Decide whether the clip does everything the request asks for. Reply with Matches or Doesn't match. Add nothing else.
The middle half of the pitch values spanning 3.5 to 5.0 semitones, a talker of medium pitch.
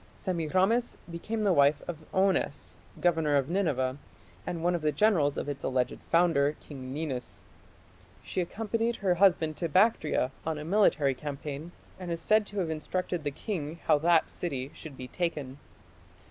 Matches